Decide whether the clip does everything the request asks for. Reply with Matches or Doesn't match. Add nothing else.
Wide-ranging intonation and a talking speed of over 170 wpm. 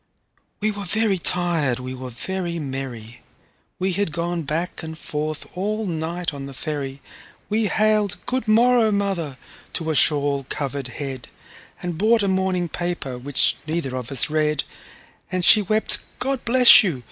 Doesn't match